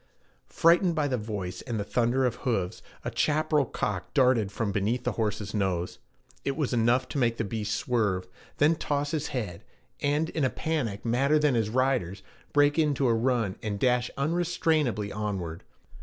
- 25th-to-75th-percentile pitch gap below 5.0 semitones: No, wide, 5.6 semitones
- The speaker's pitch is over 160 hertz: No, low, 125 Hz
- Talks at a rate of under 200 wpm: Yes, average, 170 wpm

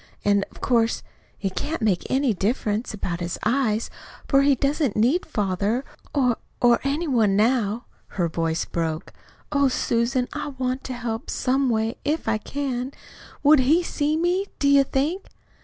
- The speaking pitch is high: Yes, high, 245 Hz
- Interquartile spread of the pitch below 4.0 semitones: No, average, 4.7 semitones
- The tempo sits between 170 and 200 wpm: No, average, 160 wpm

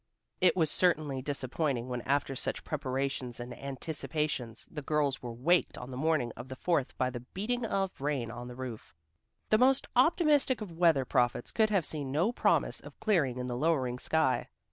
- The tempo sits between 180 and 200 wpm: Yes, average, 185 wpm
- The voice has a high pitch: No, medium, 140 Hz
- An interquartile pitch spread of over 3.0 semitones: Yes, average, 5.3 semitones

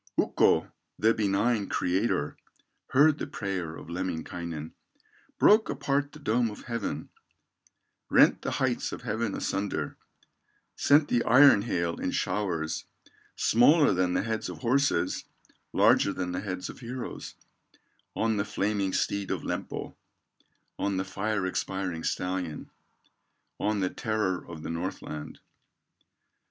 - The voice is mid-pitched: No, low, 100 Hz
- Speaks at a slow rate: Yes, slow, 125 wpm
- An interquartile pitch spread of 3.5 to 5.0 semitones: Yes, average, 4.4 semitones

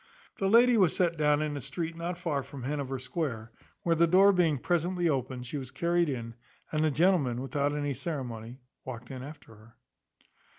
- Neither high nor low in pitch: Yes, medium, 150 Hz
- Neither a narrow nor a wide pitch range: Yes, average, 4.7 semitones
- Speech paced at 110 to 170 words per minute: No, average, 185 wpm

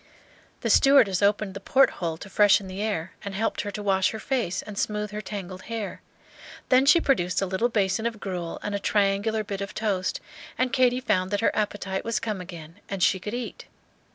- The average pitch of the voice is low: No, high, 205 Hz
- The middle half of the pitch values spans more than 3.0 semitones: No, narrow, 2.6 semitones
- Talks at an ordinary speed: No, fast, 210 wpm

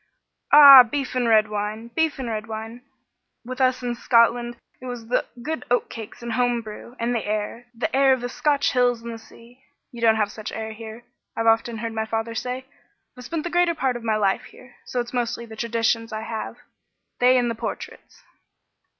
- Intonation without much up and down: Yes, narrow, 2.1 semitones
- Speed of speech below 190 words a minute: No, average, 200 wpm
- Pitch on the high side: Yes, high, 235 Hz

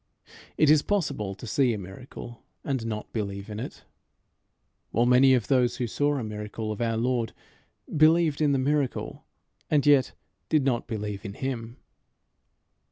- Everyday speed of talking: Yes, average, 160 wpm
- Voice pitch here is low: Yes, low, 120 Hz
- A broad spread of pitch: No, average, 4.7 semitones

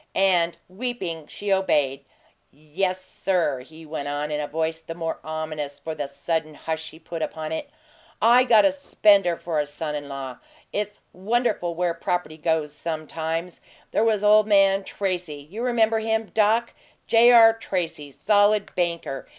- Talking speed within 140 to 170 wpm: Yes, average, 160 wpm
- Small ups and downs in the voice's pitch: No, average, 5.1 semitones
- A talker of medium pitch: Yes, medium, 170 Hz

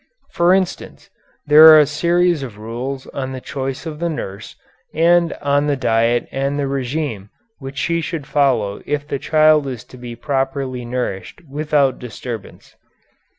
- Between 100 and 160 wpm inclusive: Yes, average, 155 wpm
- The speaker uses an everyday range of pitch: Yes, average, 3.6 semitones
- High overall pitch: No, medium, 140 Hz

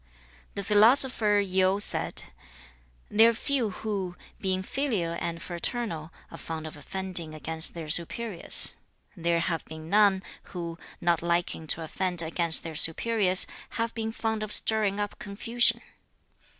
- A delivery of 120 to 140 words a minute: Yes, slow, 135 wpm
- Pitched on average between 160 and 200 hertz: Yes, high, 190 Hz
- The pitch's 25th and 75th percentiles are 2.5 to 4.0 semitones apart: No, average, 4.4 semitones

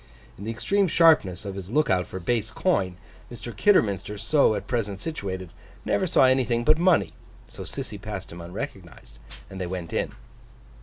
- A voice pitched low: Yes, low, 105 Hz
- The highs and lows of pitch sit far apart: Yes, wide, 6.9 semitones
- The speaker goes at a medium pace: Yes, average, 170 wpm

